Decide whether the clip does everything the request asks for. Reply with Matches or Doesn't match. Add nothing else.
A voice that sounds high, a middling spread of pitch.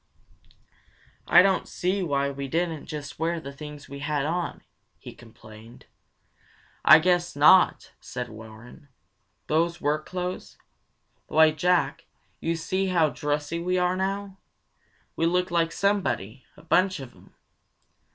Doesn't match